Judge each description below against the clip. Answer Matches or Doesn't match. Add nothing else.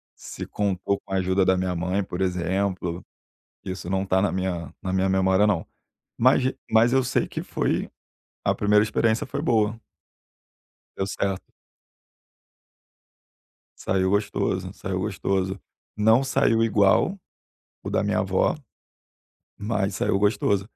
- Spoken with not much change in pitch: Matches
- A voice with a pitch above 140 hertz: Doesn't match